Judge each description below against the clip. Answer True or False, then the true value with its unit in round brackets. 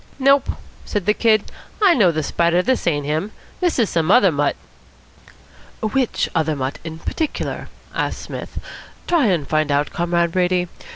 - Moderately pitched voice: True (180 Hz)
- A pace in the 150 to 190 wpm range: True (160 wpm)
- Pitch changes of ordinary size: False (6.3 semitones)